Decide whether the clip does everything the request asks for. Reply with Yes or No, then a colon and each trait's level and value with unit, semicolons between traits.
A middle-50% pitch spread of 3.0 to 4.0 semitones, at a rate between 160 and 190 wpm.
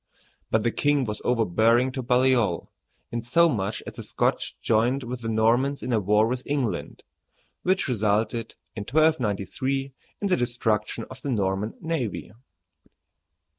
No: average, 3.6 semitones; slow, 135 wpm